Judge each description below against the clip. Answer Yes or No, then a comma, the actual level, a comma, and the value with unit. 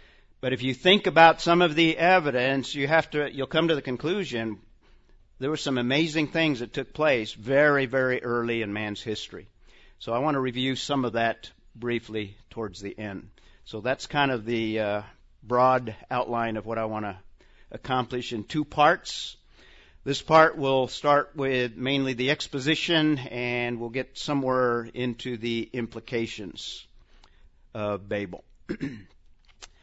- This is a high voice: No, low, 125 Hz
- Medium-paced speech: Yes, average, 155 wpm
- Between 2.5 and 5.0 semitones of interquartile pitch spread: Yes, average, 3.9 semitones